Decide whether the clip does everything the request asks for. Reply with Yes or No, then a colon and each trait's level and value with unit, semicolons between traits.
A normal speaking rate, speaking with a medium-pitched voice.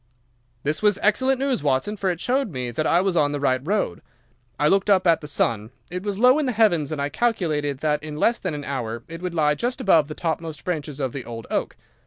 No: fast, 245 wpm; medium, 160 Hz